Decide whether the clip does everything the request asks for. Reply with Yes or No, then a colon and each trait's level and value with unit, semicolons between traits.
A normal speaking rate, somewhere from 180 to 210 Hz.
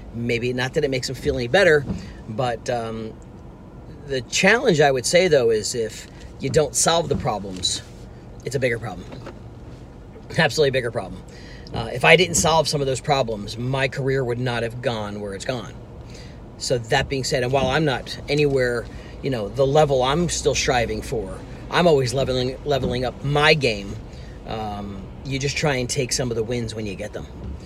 No: average, 190 wpm; low, 130 Hz